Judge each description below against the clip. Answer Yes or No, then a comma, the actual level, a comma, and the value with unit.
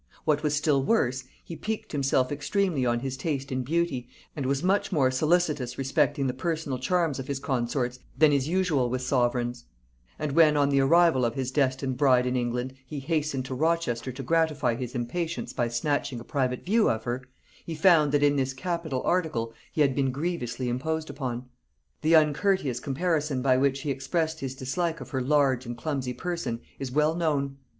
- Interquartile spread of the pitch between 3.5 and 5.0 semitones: Yes, average, 3.8 semitones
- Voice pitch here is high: No, medium, 140 Hz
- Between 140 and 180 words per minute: No, average, 190 wpm